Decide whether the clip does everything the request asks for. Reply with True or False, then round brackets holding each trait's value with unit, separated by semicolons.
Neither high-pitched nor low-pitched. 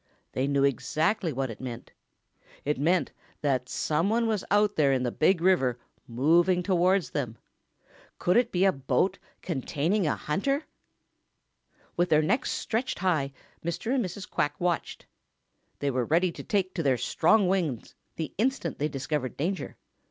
True (165 Hz)